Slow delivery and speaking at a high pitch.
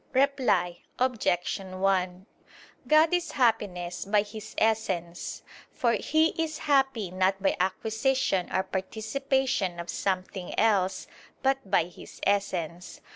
Yes: slow, 115 wpm; high, 200 Hz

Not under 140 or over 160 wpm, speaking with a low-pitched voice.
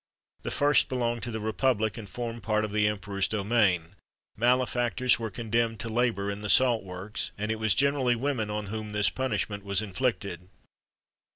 No: average, 175 wpm; low, 110 Hz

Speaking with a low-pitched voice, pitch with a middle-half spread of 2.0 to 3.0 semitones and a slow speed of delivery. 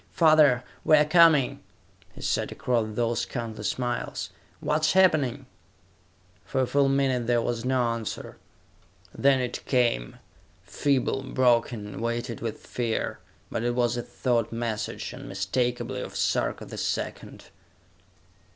Yes: low, 125 Hz; average, 2.7 semitones; slow, 130 wpm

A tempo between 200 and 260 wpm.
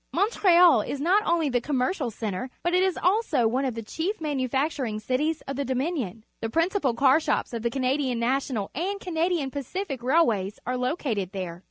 No: average, 180 wpm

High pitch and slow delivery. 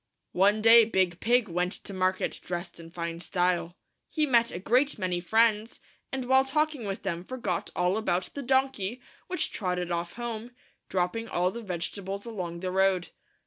No: high, 195 Hz; average, 170 wpm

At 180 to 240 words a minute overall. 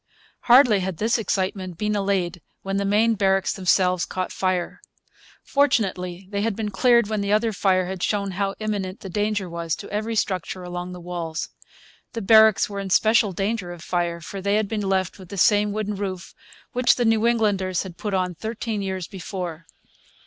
Yes: average, 185 wpm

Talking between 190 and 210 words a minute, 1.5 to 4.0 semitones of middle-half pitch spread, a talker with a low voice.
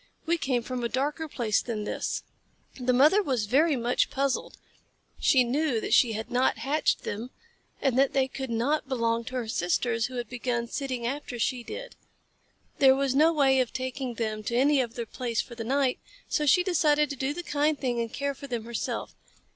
No: average, 200 wpm; average, 3.0 semitones; very high, 255 Hz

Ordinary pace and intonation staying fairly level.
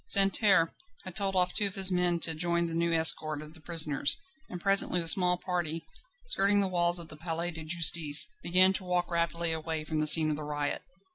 No: fast, 215 wpm; narrow, 2.2 semitones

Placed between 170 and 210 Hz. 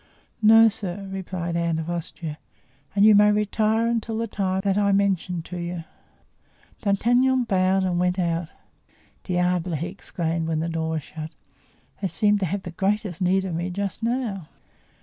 Yes: high, 190 Hz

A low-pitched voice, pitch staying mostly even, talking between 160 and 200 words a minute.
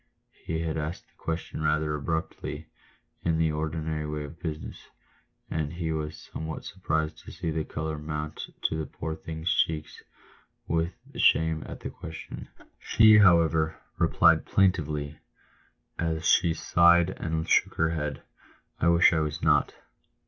No: very low, 80 Hz; narrow, 1.2 semitones; average, 150 wpm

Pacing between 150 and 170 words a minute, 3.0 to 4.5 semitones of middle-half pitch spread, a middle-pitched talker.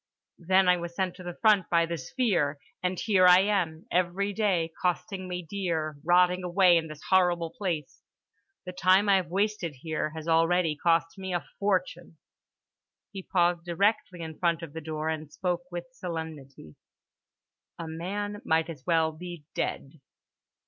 No: average, 160 wpm; narrow, 2.4 semitones; medium, 175 Hz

